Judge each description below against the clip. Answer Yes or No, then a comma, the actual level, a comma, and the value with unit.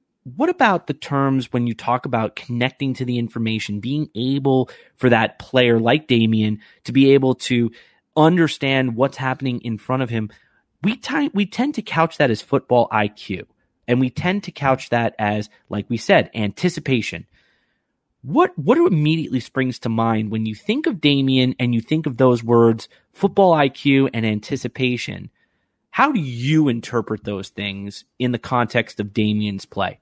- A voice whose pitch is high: No, low, 125 Hz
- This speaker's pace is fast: No, average, 170 wpm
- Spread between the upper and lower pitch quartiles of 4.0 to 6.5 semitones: Yes, average, 4.3 semitones